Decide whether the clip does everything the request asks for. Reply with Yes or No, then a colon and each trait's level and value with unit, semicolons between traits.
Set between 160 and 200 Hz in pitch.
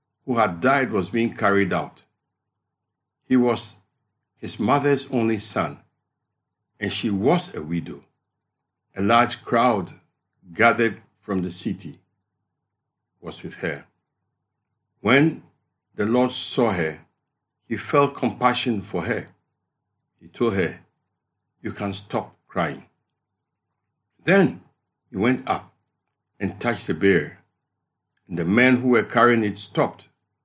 No: low, 115 Hz